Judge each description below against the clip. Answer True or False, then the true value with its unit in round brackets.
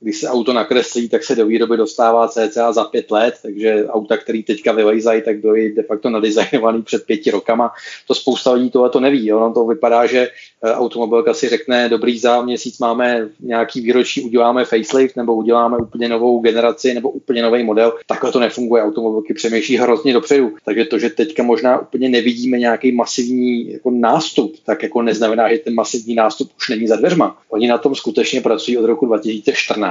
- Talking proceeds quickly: True (185 wpm)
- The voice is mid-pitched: False (120 Hz)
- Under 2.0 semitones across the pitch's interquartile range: True (1.3 semitones)